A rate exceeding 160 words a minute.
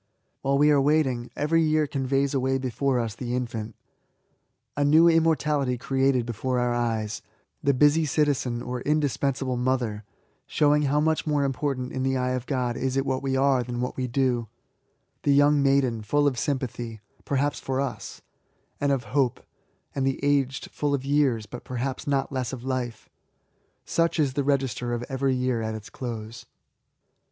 Yes: average, 175 wpm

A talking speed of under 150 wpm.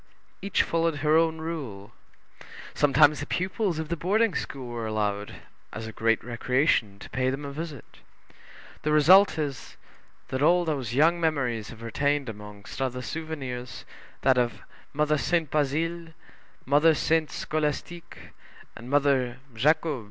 Yes: average, 140 wpm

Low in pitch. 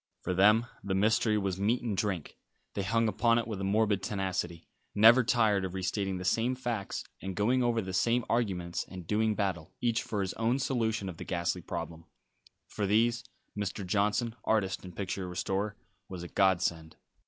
Yes: low, 100 Hz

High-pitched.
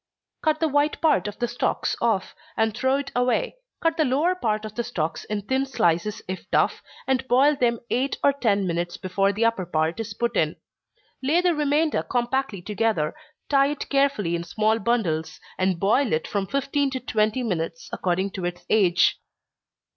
Yes: high, 230 Hz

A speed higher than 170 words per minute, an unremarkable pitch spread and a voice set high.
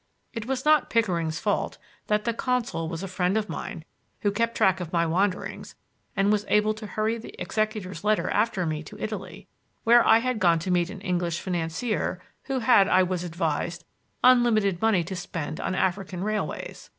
Yes: average, 185 wpm; average, 3.8 semitones; high, 195 Hz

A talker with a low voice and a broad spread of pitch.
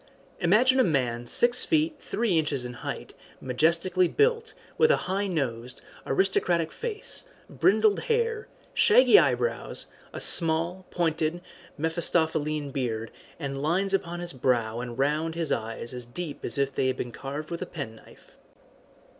No: medium, 160 Hz; wide, 6.5 semitones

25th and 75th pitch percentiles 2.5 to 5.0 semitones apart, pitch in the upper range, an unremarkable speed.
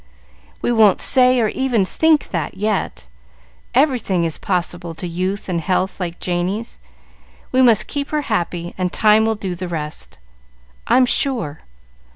No: wide, 5.5 semitones; high, 200 Hz; average, 150 wpm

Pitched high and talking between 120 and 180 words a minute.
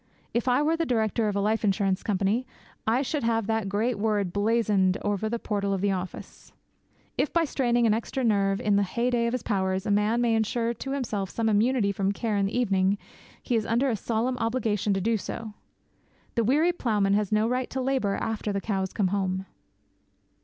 No: high, 220 Hz; fast, 205 wpm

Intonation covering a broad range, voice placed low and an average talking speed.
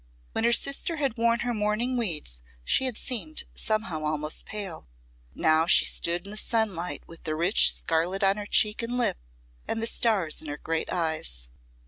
No: wide, 6.2 semitones; high, 200 Hz; average, 185 wpm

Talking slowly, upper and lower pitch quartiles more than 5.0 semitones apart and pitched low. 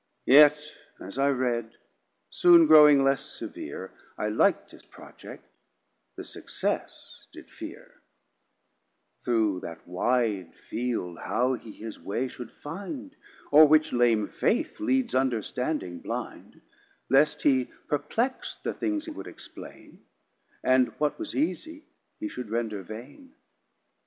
Yes: slow, 120 wpm; wide, 5.6 semitones; low, 130 Hz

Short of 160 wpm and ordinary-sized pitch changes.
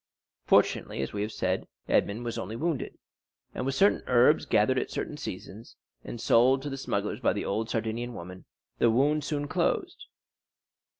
No: average, 170 wpm; average, 4.1 semitones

